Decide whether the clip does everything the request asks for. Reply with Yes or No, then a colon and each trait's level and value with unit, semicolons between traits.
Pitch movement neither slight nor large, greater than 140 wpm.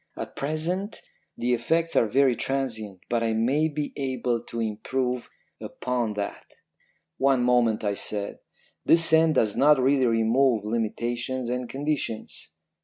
No: average, 3.4 semitones; slow, 135 wpm